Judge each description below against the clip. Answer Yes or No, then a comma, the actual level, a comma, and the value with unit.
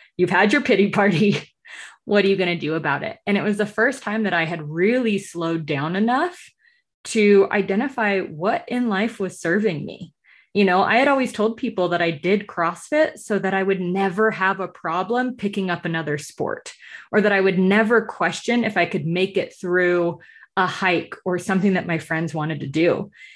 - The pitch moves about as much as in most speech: Yes, average, 4.0 semitones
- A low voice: No, high, 195 Hz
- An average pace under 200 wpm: No, fast, 205 wpm